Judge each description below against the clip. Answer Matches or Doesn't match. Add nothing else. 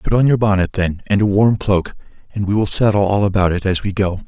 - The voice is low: Matches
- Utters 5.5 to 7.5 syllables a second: Matches